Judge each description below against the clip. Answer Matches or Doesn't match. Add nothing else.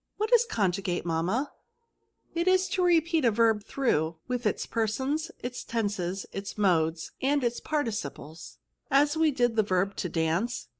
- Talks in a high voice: Matches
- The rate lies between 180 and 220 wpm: Matches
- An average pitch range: Doesn't match